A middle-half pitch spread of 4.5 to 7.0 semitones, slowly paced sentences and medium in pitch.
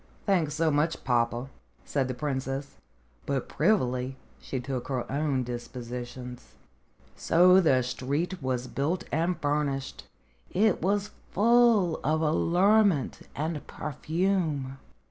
Yes: average, 5.1 semitones; slow, 110 wpm; medium, 145 Hz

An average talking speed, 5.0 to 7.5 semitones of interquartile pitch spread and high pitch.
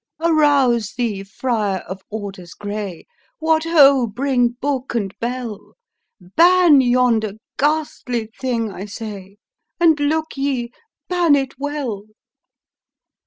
No: slow, 115 wpm; wide, 5.5 semitones; high, 245 Hz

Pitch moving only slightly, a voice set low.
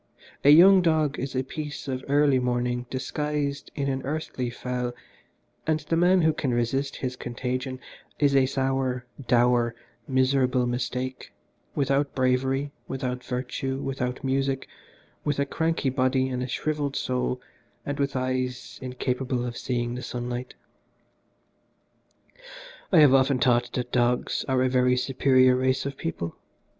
Yes: narrow, 1.8 semitones; low, 130 Hz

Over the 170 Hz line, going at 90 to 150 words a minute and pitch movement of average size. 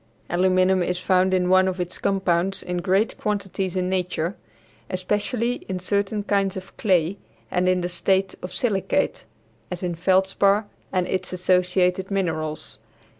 No: medium, 185 Hz; average, 145 wpm; narrow, 1.4 semitones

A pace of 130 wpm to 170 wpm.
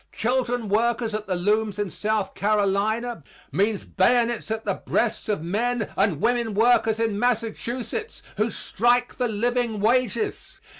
Yes: average, 140 wpm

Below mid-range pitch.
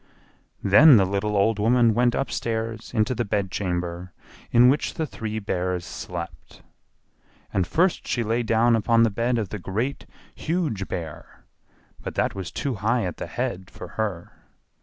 Yes: low, 110 Hz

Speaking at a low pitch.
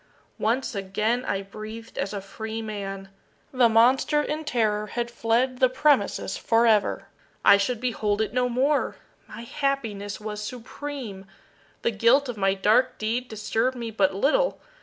No: high, 225 Hz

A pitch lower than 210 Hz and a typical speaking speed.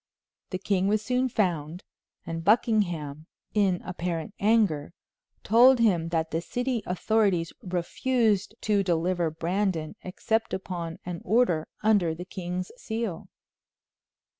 No: medium, 185 Hz; slow, 115 wpm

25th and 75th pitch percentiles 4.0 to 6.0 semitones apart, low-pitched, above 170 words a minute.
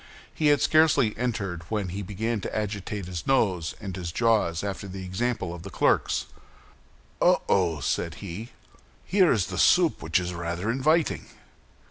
No: average, 4.9 semitones; low, 100 Hz; average, 160 wpm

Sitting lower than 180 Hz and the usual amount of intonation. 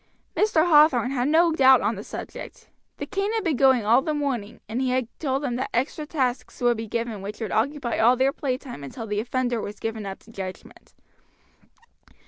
No: very high, 250 Hz; average, 4.0 semitones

